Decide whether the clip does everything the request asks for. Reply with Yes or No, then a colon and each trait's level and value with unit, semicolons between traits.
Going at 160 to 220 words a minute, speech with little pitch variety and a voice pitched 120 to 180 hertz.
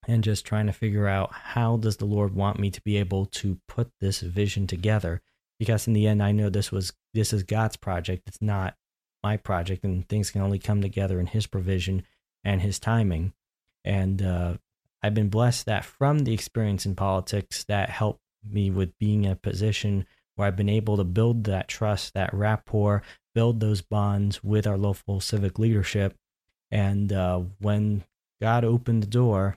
No: average, 185 wpm; narrow, 1.8 semitones; low, 100 Hz